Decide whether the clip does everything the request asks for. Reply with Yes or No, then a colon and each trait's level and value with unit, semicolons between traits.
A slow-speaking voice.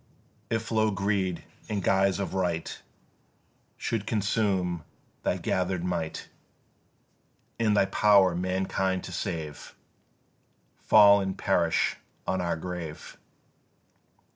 Yes: slow, 100 wpm